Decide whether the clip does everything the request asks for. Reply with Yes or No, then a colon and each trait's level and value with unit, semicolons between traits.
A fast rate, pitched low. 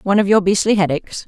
No: fast, 285 wpm; high, 190 Hz